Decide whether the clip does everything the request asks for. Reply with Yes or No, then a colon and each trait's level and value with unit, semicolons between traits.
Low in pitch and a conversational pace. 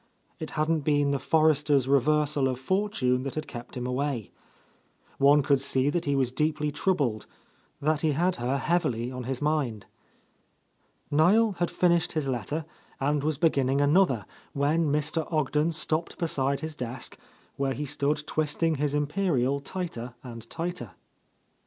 No: medium, 145 Hz; average, 150 wpm